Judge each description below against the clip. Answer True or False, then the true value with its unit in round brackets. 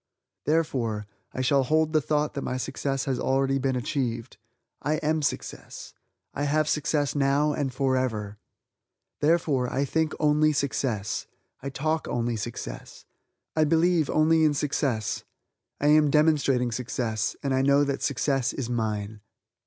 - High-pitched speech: False (140 Hz)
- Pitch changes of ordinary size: True (3.3 semitones)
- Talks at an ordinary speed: True (145 wpm)